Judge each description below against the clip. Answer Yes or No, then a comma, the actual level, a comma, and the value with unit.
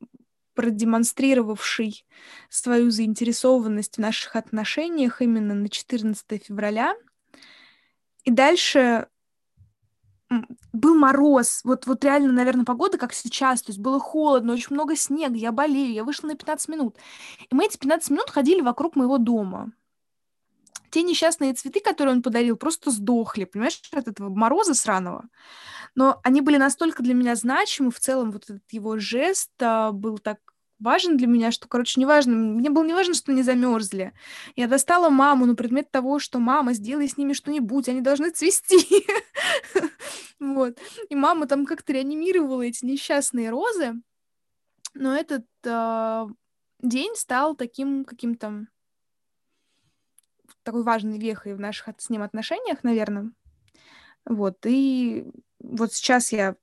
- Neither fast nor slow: Yes, average, 135 wpm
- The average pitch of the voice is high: Yes, very high, 255 Hz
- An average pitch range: Yes, average, 4.1 semitones